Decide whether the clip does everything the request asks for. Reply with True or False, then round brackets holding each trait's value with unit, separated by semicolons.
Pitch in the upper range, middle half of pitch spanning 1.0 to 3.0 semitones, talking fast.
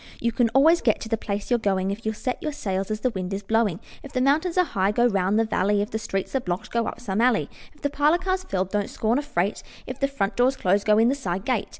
False (220 Hz; 4.8 semitones; 285 wpm)